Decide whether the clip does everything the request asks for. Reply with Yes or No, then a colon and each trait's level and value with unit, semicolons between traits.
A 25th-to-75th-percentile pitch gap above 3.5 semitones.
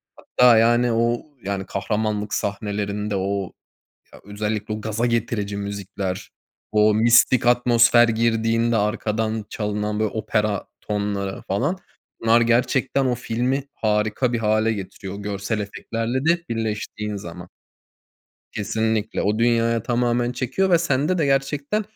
No: narrow, 2.4 semitones